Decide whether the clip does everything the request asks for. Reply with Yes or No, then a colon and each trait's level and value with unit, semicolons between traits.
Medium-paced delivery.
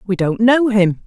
No: fast, 225 wpm